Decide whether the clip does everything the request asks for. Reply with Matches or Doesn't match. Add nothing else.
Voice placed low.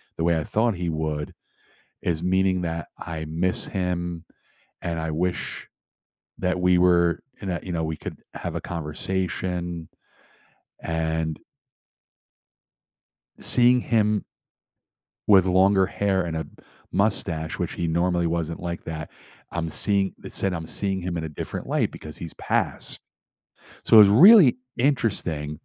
Matches